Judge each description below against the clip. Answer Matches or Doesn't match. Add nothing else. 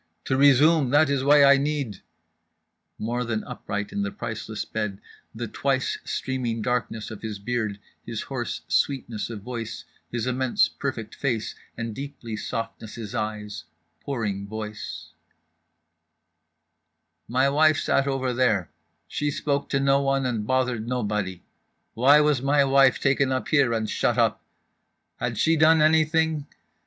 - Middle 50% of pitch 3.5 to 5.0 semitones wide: Matches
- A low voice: Matches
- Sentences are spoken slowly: Matches